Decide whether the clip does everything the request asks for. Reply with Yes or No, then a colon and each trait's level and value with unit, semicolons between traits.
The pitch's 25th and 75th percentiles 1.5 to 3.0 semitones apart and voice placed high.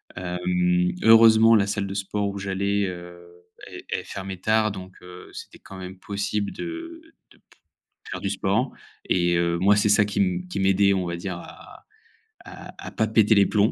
No: narrow, 2.4 semitones; low, 100 Hz